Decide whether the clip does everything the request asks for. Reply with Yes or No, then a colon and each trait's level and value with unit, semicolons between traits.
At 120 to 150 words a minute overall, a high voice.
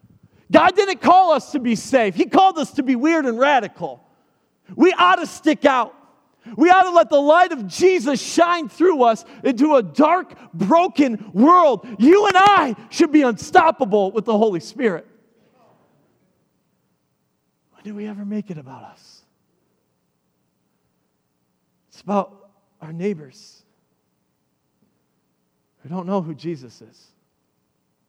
Yes: slow, 135 wpm; high, 245 Hz